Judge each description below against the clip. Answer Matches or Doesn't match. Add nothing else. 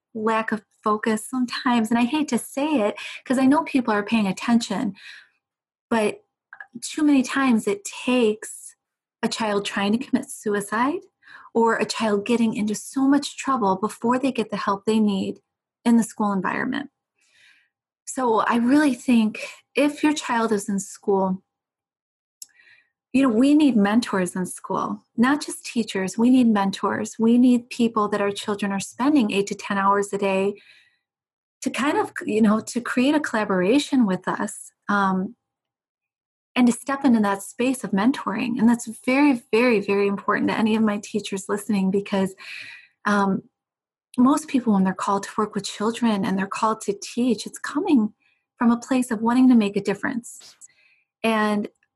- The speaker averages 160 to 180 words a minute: Matches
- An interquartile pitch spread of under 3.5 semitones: Doesn't match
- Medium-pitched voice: Doesn't match